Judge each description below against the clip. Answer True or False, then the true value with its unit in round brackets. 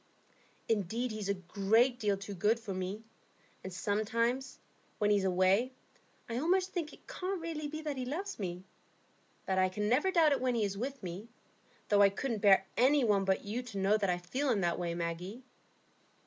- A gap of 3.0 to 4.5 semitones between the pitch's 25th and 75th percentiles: False (5.1 semitones)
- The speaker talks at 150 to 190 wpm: False (200 wpm)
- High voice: True (215 Hz)